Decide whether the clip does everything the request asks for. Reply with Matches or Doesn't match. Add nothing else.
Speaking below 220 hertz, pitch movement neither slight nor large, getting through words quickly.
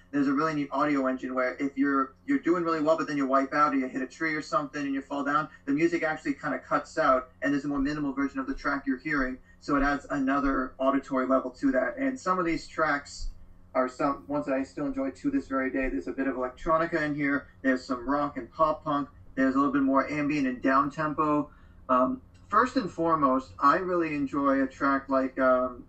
Matches